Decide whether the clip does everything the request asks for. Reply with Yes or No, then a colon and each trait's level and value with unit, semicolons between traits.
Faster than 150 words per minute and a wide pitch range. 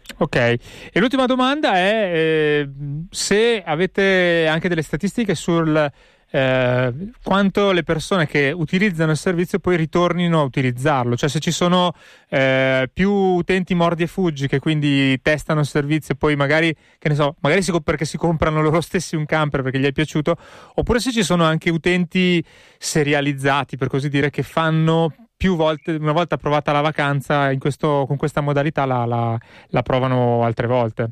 No: fast, 170 wpm; average, 3.8 semitones